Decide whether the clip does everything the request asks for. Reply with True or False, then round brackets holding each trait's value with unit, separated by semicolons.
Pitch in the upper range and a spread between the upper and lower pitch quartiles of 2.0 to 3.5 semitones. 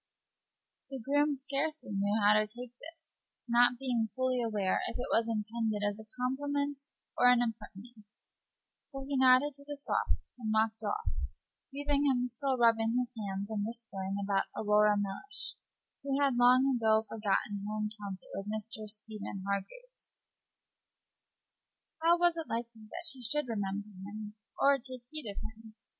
False (230 Hz; 4.3 semitones)